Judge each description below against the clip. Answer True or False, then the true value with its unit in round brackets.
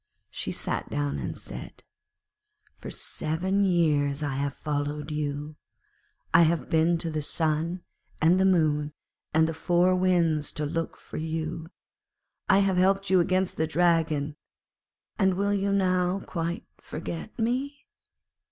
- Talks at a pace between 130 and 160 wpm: True (140 wpm)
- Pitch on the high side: False (165 Hz)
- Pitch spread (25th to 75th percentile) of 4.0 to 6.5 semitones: False (3.4 semitones)